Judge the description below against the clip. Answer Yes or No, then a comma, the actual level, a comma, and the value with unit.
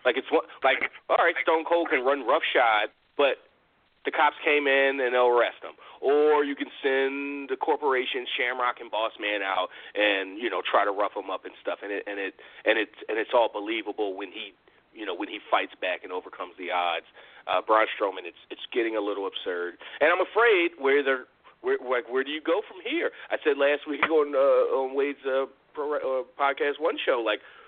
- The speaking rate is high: Yes, fast, 225 wpm